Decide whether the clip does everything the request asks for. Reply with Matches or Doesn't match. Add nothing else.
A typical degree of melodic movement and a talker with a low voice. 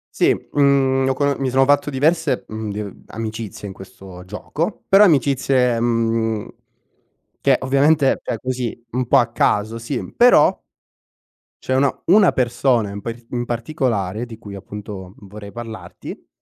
Matches